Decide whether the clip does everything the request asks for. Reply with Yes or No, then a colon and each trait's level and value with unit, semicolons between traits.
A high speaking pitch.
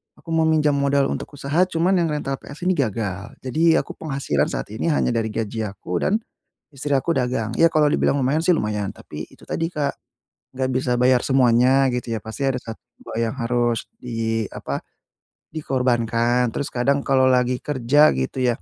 No: low, 130 Hz